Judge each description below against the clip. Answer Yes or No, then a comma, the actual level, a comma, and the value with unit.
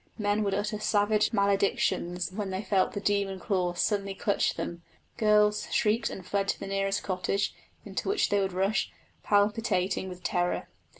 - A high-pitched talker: Yes, high, 200 Hz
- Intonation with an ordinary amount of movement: No, narrow, 1.7 semitones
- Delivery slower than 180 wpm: Yes, average, 165 wpm